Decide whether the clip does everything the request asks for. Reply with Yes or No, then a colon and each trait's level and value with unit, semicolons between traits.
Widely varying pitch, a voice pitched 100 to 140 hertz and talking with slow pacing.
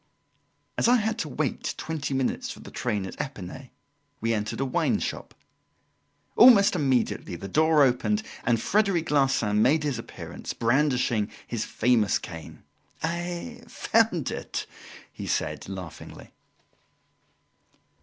Yes: wide, 6.9 semitones; low, 135 Hz; slow, 125 wpm